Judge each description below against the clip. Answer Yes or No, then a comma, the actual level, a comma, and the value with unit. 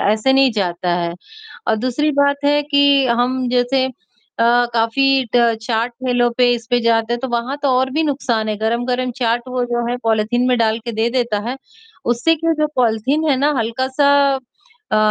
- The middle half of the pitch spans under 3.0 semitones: Yes, narrow, 2.6 semitones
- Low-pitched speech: No, high, 245 Hz